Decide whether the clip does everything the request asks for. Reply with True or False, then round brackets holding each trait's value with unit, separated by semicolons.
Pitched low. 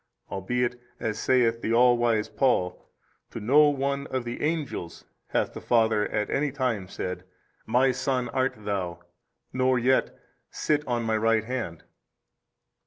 True (120 Hz)